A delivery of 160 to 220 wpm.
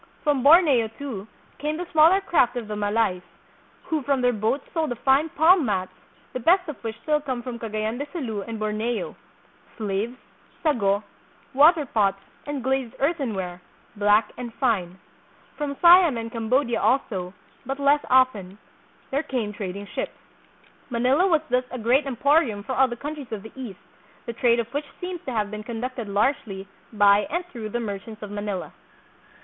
Yes: average, 170 wpm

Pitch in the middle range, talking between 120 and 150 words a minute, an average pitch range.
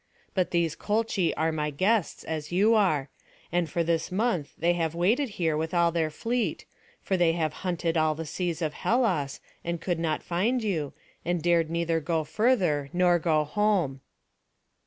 No: medium, 170 Hz; average, 175 wpm; average, 3.0 semitones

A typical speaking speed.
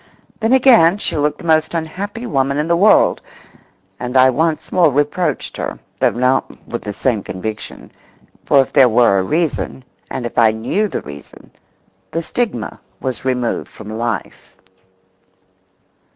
Yes: average, 150 wpm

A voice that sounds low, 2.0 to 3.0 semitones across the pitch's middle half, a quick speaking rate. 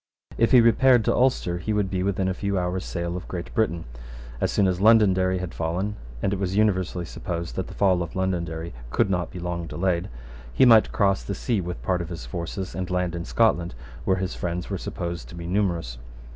Yes: very low, 90 Hz; narrow, 2.4 semitones; fast, 215 wpm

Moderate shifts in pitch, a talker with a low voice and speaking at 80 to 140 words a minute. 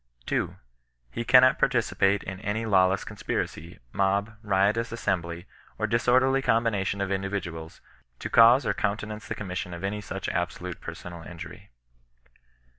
Yes: average, 3.7 semitones; low, 100 Hz; slow, 135 wpm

